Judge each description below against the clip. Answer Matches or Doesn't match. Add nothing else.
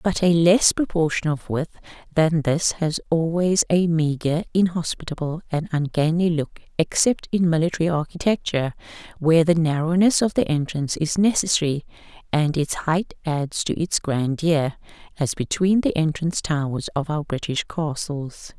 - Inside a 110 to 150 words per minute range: Matches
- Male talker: Doesn't match